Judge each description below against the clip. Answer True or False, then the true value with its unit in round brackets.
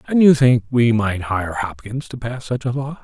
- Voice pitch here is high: False (120 Hz)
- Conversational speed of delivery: False (240 wpm)